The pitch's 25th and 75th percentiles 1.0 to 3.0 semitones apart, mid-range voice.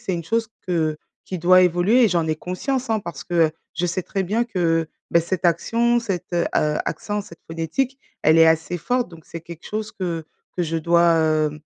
No: average, 4.1 semitones; medium, 175 Hz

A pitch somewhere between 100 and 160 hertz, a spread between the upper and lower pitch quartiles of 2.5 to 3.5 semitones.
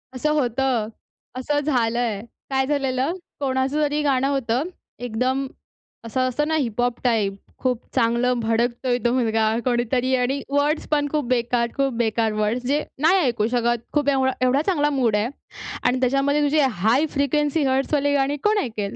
No: very high, 255 Hz; average, 3.2 semitones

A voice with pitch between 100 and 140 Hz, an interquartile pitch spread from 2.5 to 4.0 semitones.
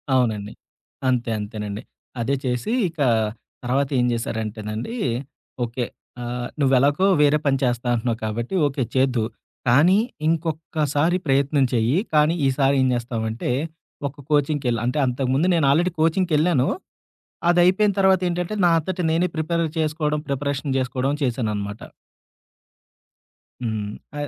No: low, 135 Hz; average, 4.6 semitones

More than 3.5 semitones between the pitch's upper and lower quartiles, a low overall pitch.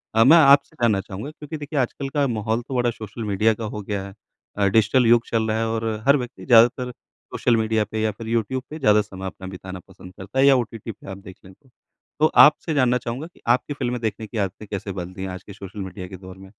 Yes: average, 4.3 semitones; low, 110 Hz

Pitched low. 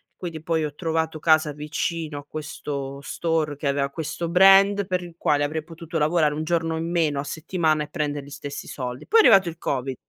No: medium, 160 Hz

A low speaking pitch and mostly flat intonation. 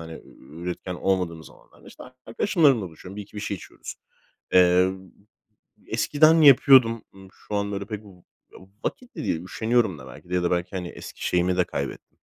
No: very low, 95 Hz; average, 4.4 semitones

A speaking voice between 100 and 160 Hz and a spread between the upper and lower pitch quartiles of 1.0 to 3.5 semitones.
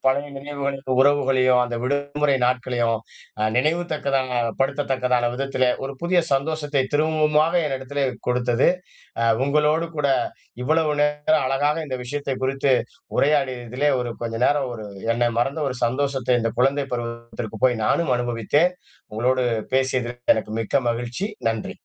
Yes: low, 135 Hz; average, 2.9 semitones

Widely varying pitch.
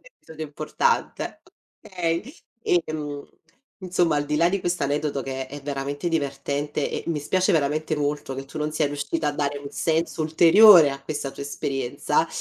No: narrow, 2.6 semitones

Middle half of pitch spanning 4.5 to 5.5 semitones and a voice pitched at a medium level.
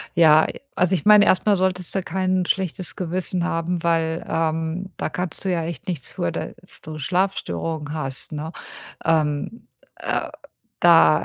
No: average, 2.8 semitones; medium, 170 Hz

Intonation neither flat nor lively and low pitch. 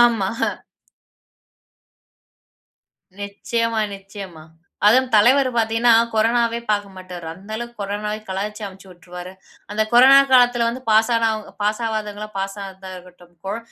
No: average, 3.2 semitones; high, 210 Hz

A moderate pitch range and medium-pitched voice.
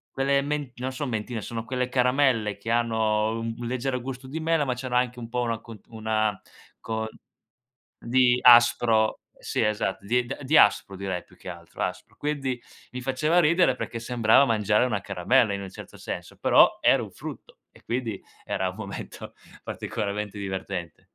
No: average, 3.2 semitones; low, 120 Hz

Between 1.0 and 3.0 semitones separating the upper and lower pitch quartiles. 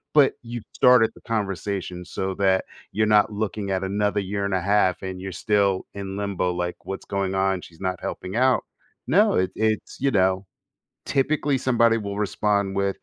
Yes: narrow, 2.5 semitones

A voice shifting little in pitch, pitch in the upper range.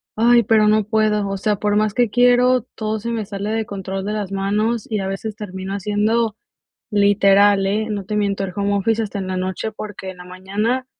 Yes: narrow, 1.9 semitones; high, 210 Hz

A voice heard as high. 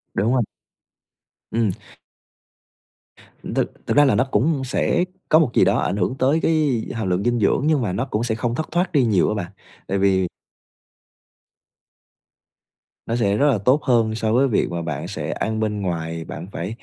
No: low, 115 Hz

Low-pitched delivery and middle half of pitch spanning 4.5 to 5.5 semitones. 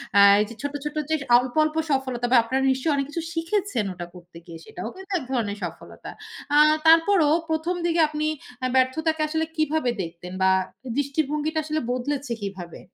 No: very high, 285 Hz; average, 5.2 semitones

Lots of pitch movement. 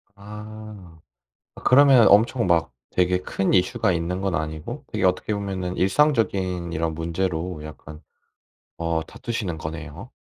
No: average, 3.9 semitones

